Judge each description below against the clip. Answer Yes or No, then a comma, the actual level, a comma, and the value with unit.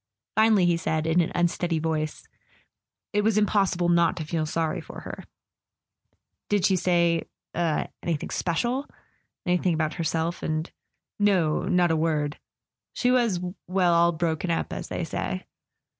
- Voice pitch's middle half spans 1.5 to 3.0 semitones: Yes, narrow, 2.4 semitones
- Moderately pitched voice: Yes, medium, 170 Hz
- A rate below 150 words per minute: Yes, average, 140 wpm